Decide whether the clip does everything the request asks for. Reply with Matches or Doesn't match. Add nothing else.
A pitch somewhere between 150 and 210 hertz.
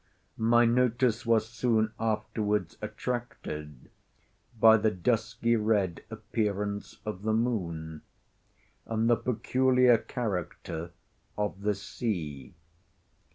Doesn't match